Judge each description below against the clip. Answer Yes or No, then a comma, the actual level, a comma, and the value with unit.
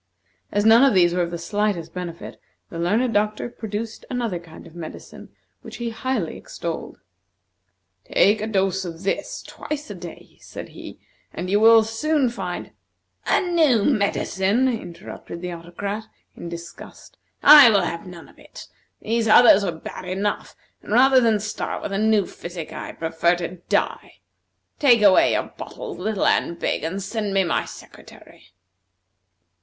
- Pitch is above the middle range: Yes, high, 205 Hz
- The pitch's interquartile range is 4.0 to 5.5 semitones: Yes, average, 4.4 semitones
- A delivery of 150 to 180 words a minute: Yes, average, 160 wpm